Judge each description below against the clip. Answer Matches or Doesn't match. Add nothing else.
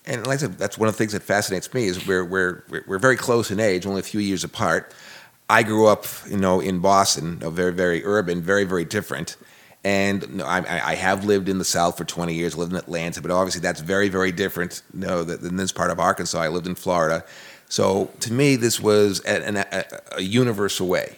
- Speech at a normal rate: Doesn't match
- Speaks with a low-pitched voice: Matches